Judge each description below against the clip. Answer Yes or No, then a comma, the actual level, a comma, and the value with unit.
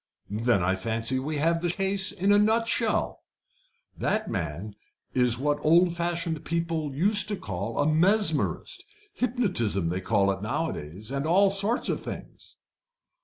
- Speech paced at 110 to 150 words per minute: Yes, average, 145 wpm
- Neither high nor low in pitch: Yes, medium, 155 Hz